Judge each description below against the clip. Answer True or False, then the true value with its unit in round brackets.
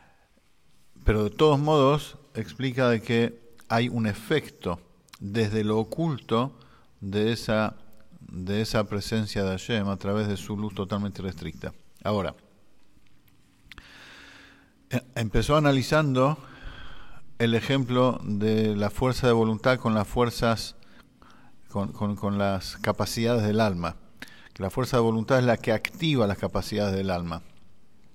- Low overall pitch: True (110 Hz)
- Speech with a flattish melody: False (3.3 semitones)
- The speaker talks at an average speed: False (130 wpm)